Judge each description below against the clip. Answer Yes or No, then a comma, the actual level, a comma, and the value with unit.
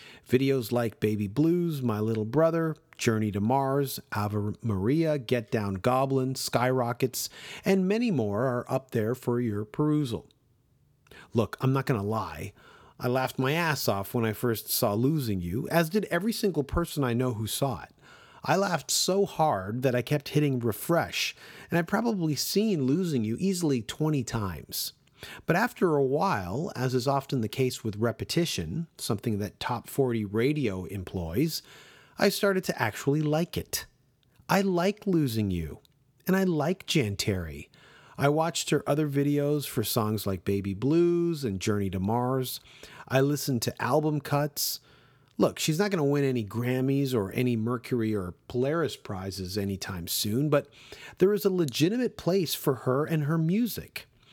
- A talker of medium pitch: No, low, 130 Hz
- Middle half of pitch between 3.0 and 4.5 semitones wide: No, wide, 5.5 semitones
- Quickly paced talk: No, average, 160 wpm